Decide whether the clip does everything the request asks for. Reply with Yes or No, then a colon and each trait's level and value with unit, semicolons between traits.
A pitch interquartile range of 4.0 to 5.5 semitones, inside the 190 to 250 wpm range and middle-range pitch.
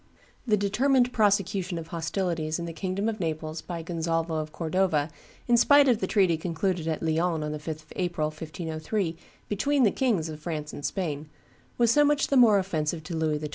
Yes: average, 4.5 semitones; average, 200 wpm; medium, 170 Hz